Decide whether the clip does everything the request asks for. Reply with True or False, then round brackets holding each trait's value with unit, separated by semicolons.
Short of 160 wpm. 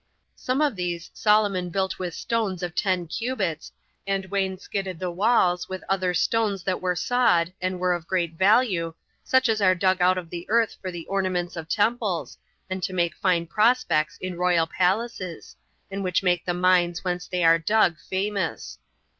False (175 wpm)